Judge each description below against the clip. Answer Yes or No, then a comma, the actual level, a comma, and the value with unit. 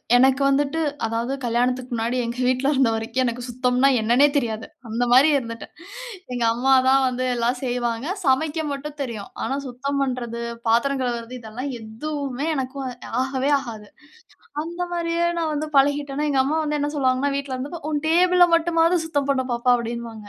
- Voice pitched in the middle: No, very high, 260 Hz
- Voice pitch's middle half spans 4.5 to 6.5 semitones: No, average, 3.2 semitones